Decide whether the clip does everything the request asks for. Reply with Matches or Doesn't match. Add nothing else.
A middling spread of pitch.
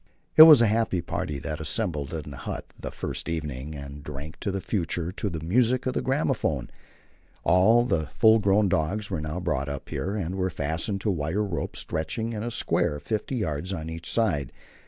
Doesn't match